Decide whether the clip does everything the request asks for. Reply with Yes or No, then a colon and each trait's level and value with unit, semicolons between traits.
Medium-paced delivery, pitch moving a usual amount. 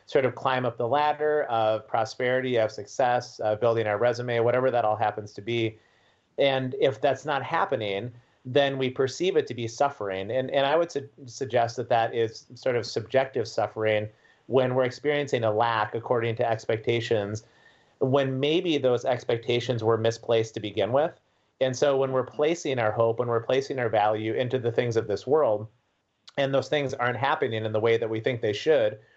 Yes: average, 190 wpm; average, 3.1 semitones